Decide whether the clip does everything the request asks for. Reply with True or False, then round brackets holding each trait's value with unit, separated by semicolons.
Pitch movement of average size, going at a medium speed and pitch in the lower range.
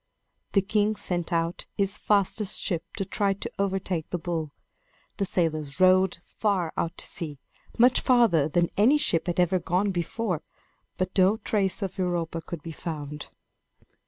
False (3.1 semitones; 160 wpm; 185 Hz)